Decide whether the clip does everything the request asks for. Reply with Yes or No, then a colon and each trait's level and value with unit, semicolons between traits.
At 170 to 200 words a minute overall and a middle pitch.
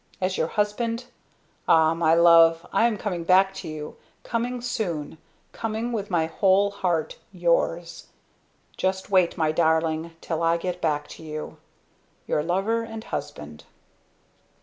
No: average, 140 wpm; medium, 175 Hz